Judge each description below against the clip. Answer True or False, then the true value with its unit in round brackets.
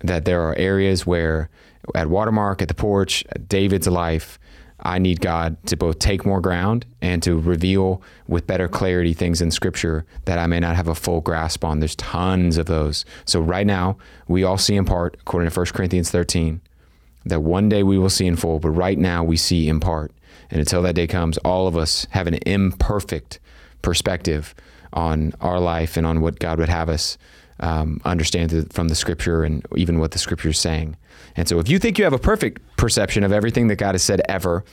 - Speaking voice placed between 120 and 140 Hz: False (85 Hz)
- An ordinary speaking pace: False (215 wpm)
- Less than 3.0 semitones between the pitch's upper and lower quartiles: True (2.4 semitones)